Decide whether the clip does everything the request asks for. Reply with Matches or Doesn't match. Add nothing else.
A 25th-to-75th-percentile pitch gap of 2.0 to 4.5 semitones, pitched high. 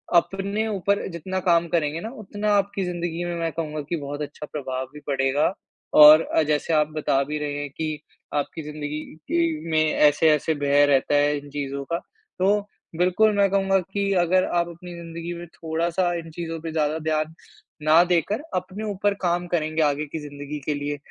Doesn't match